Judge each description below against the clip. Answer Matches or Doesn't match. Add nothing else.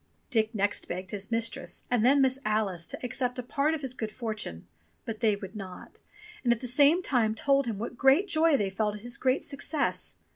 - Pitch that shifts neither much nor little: Matches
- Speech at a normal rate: Doesn't match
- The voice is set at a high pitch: Matches